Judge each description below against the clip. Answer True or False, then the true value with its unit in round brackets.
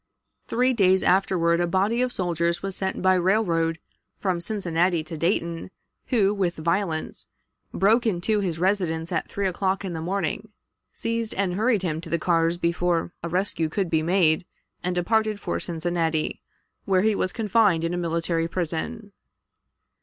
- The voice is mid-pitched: True (180 Hz)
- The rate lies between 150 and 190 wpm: True (160 wpm)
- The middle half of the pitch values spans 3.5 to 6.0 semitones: False (3.0 semitones)